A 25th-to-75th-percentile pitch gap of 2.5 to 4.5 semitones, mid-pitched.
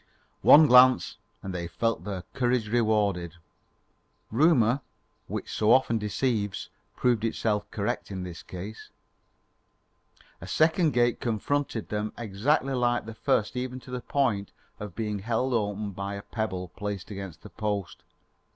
No: average, 3.8 semitones; low, 110 Hz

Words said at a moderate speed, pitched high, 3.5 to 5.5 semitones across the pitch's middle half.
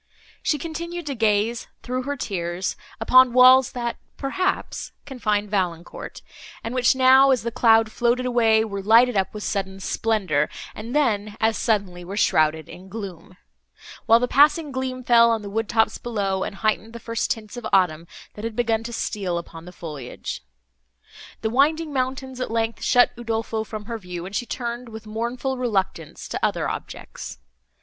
Yes: average, 170 wpm; high, 225 Hz; average, 4.0 semitones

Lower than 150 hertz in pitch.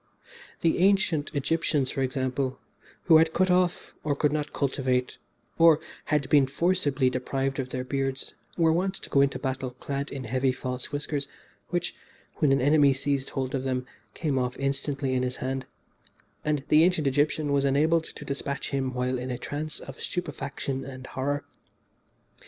Yes: medium, 140 Hz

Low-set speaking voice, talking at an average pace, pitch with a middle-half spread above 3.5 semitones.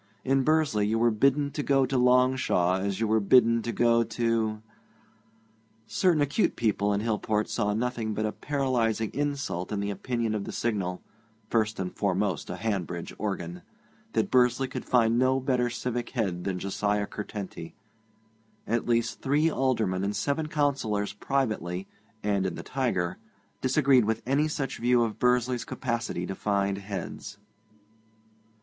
Yes: low, 115 Hz; average, 155 wpm; average, 4.1 semitones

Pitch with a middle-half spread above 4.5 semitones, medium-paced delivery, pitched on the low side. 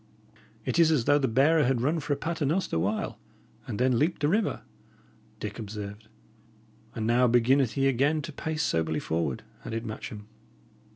Yes: wide, 5.6 semitones; average, 170 wpm; low, 130 Hz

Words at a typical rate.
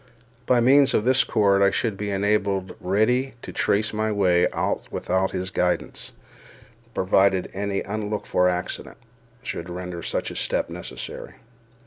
Yes: average, 145 wpm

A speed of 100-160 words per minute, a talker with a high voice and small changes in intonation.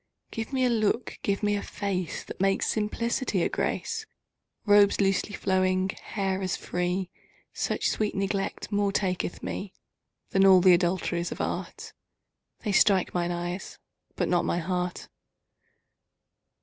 Yes: average, 140 wpm; high, 195 Hz; narrow, 2.1 semitones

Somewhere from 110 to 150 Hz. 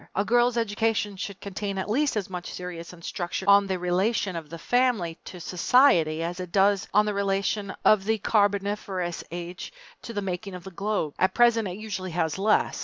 No: high, 195 Hz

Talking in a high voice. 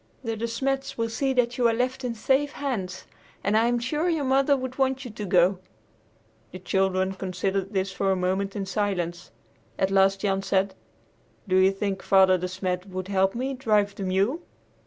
Yes: high, 200 Hz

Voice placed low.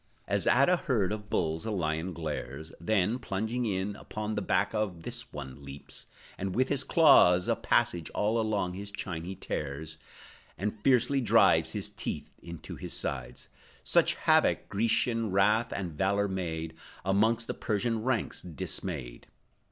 Yes: low, 100 Hz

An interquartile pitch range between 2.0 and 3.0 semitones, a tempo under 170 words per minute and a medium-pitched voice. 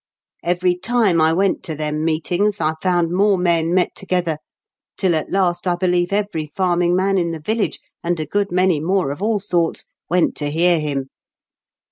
No: average, 2.7 semitones; average, 185 wpm; medium, 175 Hz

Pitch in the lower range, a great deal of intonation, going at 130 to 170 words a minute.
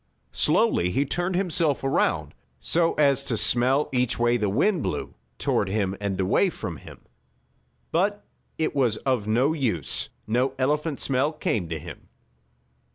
Yes: low, 130 Hz; wide, 6.0 semitones; average, 145 wpm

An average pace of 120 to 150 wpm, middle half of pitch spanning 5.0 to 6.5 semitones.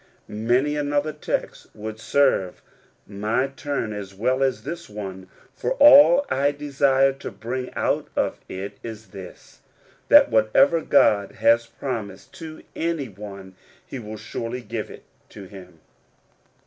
Yes: average, 140 wpm; wide, 5.4 semitones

